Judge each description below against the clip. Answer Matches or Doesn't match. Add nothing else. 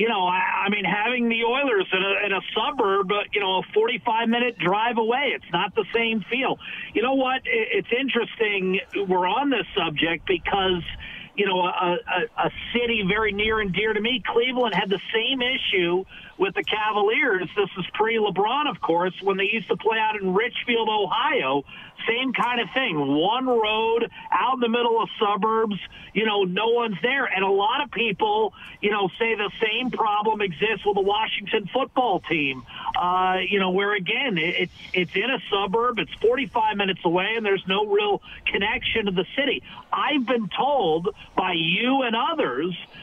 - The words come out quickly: Doesn't match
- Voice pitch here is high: Matches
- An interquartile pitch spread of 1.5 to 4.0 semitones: Doesn't match